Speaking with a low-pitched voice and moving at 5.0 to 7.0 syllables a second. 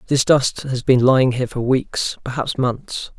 No: low, 130 Hz; 4.5 syllables/s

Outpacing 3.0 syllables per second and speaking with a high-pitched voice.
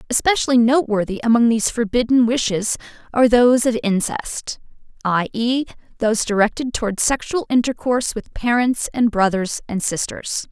Yes: 5.4 syllables/s; high, 235 Hz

